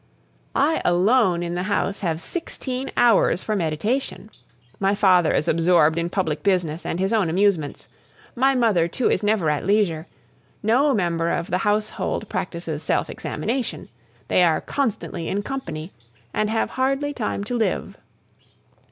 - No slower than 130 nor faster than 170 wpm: Yes, average, 150 wpm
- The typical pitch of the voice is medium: No, high, 195 Hz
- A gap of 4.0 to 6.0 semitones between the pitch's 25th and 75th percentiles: Yes, average, 5.1 semitones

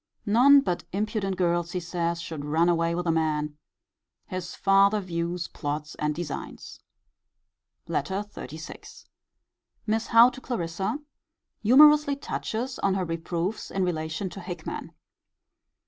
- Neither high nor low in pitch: Yes, medium, 180 Hz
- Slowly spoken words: Yes, slow, 125 wpm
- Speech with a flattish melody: No, average, 4.1 semitones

